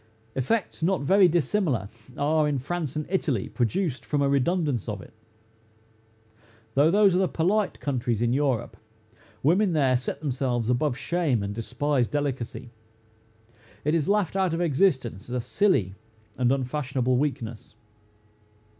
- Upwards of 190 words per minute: No, average, 140 wpm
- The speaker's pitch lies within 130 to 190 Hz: Yes, medium, 140 Hz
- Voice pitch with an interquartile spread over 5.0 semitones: Yes, wide, 5.6 semitones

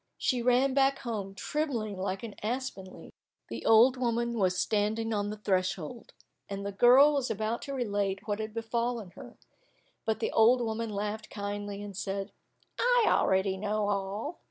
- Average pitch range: Yes, average, 3.2 semitones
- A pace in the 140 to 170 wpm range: Yes, average, 165 wpm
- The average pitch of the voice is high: Yes, high, 215 Hz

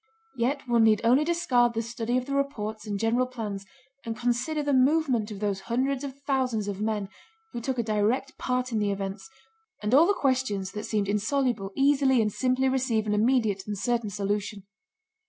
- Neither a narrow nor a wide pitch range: Yes, average, 4.0 semitones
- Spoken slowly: No, average, 190 wpm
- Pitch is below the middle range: No, high, 235 Hz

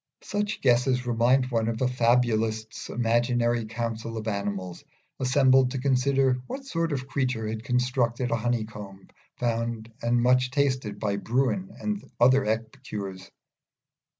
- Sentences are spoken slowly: Yes, slow, 130 wpm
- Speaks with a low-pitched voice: Yes, low, 120 Hz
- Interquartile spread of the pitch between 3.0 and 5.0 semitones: No, narrow, 2.6 semitones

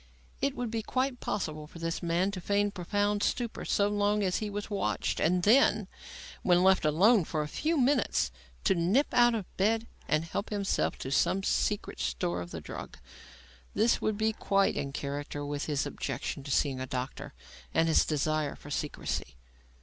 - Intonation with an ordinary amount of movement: No, wide, 6.1 semitones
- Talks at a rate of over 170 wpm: Yes, average, 180 wpm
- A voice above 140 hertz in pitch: Yes, medium, 185 Hz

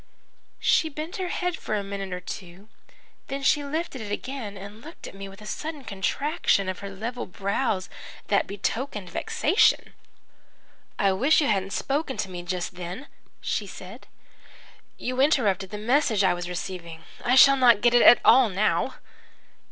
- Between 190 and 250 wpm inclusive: No, average, 165 wpm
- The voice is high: Yes, high, 210 Hz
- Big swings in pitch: Yes, wide, 6.1 semitones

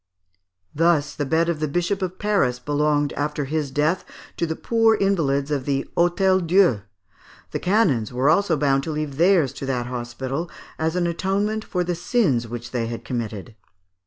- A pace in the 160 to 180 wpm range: Yes, average, 175 wpm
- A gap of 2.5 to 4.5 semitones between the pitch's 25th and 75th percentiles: No, average, 4.9 semitones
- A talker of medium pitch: Yes, medium, 155 Hz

